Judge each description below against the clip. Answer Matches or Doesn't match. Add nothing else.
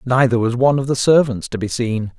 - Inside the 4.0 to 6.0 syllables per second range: Matches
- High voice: Doesn't match